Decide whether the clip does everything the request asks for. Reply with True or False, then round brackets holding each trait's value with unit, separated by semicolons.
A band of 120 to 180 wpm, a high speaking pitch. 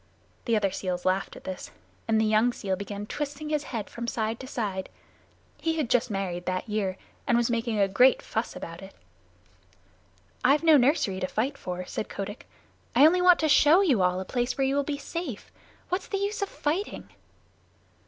False (195 wpm; 235 Hz)